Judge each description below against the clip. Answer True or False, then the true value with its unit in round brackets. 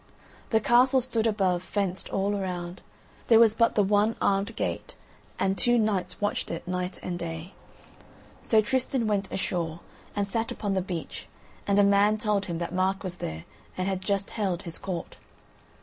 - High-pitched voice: True (195 Hz)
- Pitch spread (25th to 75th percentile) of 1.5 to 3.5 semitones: True (2.9 semitones)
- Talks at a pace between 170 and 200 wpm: True (175 wpm)